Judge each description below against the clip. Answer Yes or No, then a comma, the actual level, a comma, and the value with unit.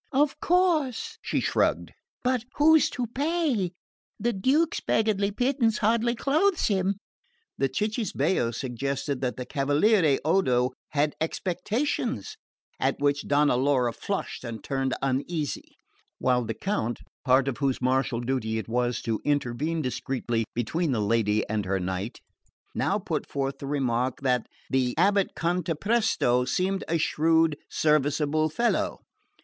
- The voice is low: No, medium, 145 Hz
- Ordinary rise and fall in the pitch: No, wide, 8.7 semitones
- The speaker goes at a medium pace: No, slow, 130 wpm